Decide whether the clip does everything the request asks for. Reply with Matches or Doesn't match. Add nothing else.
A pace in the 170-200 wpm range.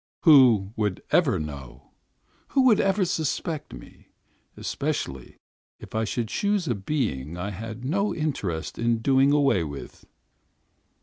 Doesn't match